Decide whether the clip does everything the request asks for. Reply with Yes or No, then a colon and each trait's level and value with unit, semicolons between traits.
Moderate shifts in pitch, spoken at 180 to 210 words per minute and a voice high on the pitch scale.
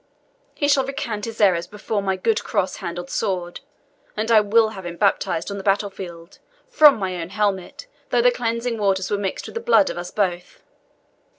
Yes: average, 3.7 semitones; average, 195 wpm; high, 205 Hz